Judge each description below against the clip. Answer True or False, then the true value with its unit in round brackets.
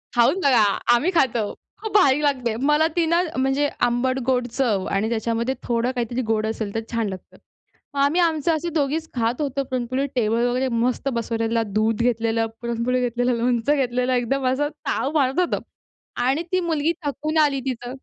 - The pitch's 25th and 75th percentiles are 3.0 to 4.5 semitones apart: True (3.4 semitones)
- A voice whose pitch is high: True (250 Hz)